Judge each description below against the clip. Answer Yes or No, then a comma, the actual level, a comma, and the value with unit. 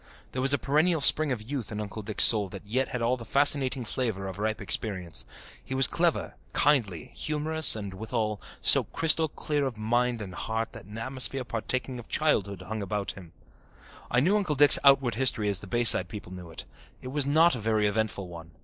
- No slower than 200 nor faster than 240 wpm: Yes, fast, 205 wpm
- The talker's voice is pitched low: Yes, low, 115 Hz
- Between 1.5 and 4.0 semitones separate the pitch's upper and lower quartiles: No, average, 4.9 semitones